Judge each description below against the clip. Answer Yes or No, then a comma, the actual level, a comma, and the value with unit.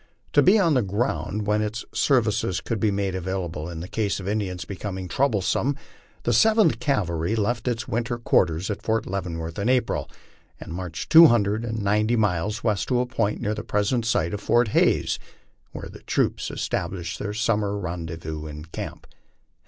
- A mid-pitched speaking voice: No, low, 105 Hz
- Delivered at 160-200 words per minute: Yes, average, 175 wpm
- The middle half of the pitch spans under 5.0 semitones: Yes, average, 4.4 semitones